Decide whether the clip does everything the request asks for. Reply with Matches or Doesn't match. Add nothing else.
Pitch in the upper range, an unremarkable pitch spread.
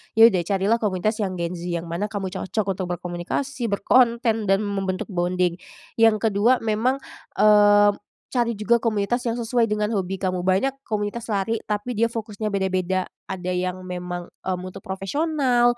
Matches